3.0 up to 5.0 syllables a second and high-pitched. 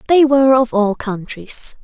Yes: 4.3 syllables/s; high, 240 Hz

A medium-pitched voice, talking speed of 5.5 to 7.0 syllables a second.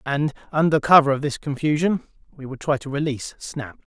Yes: medium, 145 Hz; 5.6 syllables/s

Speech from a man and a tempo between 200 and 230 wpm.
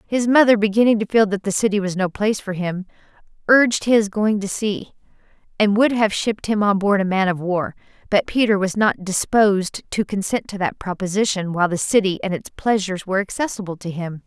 No: female; fast, 205 wpm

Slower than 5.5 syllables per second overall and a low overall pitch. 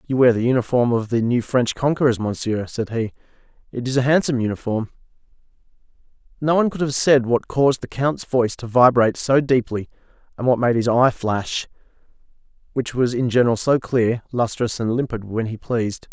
No: 5.6 syllables/s; low, 120 Hz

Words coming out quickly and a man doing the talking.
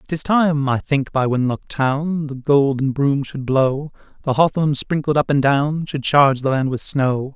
No: average, 195 wpm; male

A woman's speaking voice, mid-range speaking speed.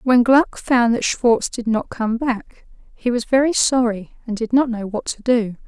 No: female; fast, 210 wpm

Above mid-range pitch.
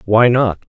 No: low, 110 Hz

